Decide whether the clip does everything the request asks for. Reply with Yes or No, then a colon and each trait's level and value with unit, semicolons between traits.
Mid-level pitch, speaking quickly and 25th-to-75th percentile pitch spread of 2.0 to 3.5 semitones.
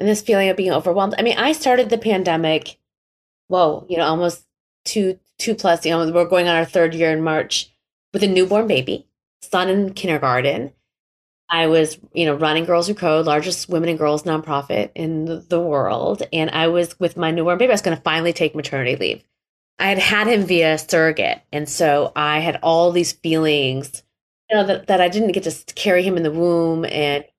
Yes: medium, 170 Hz; fast, 210 wpm; average, 3.0 semitones